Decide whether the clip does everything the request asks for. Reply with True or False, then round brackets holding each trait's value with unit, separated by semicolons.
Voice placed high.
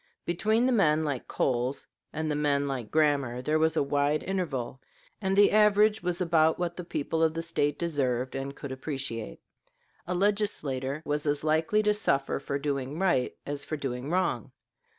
False (150 Hz)